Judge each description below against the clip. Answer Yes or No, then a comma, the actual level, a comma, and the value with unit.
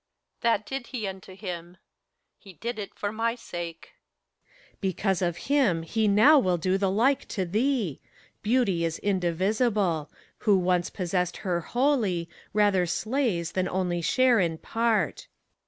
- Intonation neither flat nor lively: Yes, average, 4.6 semitones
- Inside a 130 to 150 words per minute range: Yes, average, 145 wpm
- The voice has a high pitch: Yes, high, 195 Hz